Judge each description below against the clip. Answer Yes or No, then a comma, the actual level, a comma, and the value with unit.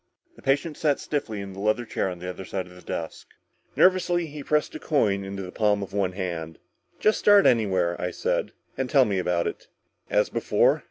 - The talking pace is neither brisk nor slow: No, fast, 215 wpm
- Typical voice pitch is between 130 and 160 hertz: No, low, 100 Hz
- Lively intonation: Yes, wide, 7.6 semitones